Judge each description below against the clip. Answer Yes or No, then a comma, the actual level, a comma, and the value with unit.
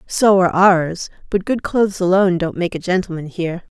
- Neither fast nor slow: Yes, average, 190 wpm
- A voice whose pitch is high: No, medium, 180 Hz